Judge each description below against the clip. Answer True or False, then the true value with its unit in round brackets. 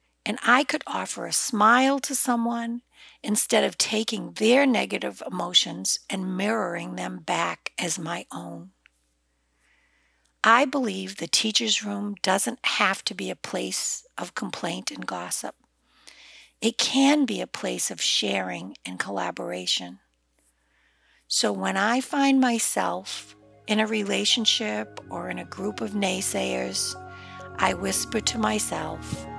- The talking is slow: True (130 wpm)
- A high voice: True (205 Hz)